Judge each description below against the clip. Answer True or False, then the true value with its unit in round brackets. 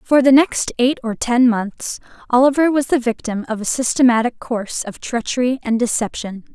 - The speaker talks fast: False (175 wpm)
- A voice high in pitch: True (245 Hz)